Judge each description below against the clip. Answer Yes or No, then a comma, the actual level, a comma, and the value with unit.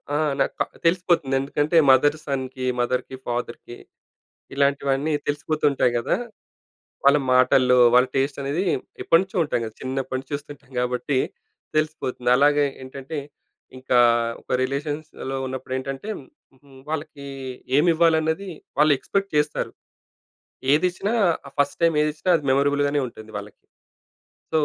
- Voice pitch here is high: No, medium, 140 Hz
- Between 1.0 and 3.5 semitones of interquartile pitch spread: Yes, average, 2.8 semitones